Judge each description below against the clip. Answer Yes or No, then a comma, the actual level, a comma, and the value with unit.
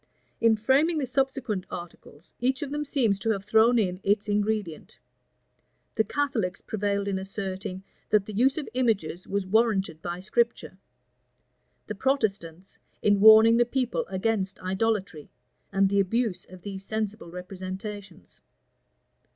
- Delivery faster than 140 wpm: No, slow, 135 wpm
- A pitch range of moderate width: Yes, average, 3.4 semitones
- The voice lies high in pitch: Yes, high, 205 Hz